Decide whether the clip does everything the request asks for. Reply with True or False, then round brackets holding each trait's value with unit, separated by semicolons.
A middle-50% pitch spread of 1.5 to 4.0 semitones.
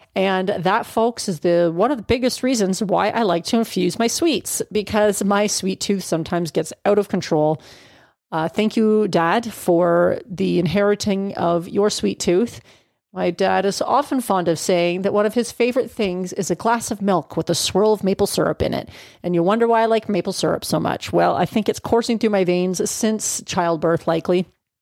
True (3.7 semitones)